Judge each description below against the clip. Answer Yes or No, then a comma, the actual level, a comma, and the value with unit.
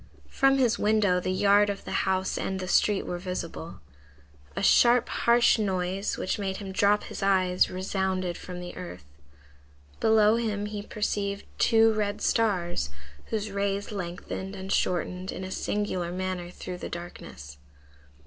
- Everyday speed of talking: Yes, average, 150 wpm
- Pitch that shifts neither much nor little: No, narrow, 2.3 semitones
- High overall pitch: Yes, high, 195 Hz